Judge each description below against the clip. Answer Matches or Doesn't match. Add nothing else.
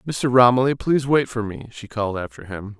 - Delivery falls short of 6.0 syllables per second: Matches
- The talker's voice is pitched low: Matches